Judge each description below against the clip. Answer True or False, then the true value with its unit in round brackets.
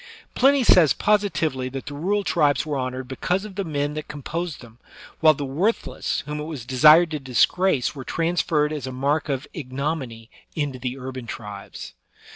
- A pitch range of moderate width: True (4.2 semitones)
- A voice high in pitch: False (145 Hz)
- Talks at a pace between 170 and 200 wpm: True (180 wpm)